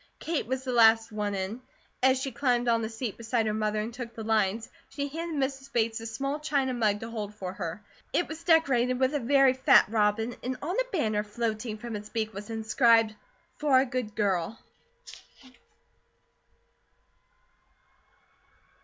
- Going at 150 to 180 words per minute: Yes, average, 170 wpm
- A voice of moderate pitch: No, high, 230 Hz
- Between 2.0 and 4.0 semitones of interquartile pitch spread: Yes, average, 3.5 semitones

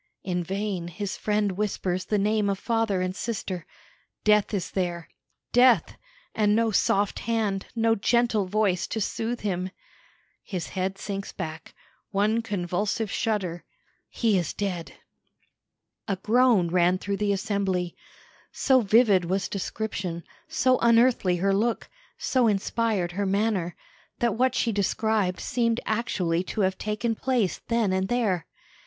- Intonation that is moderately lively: Yes, average, 3.4 semitones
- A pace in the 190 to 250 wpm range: No, slow, 135 wpm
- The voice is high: Yes, high, 205 Hz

